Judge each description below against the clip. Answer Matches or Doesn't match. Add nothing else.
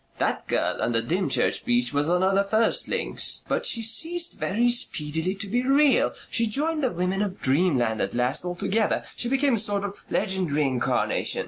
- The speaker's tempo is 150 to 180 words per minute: Doesn't match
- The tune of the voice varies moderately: Doesn't match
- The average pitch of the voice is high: Matches